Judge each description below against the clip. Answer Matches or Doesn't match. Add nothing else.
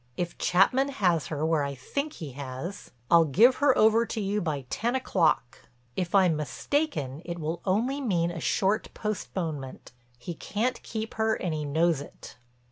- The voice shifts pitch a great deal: Matches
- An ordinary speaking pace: Matches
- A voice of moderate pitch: Matches